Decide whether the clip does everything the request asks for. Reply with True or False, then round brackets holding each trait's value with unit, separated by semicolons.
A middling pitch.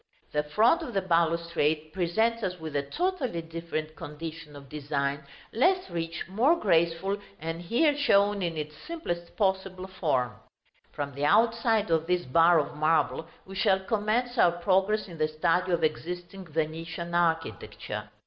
True (170 Hz)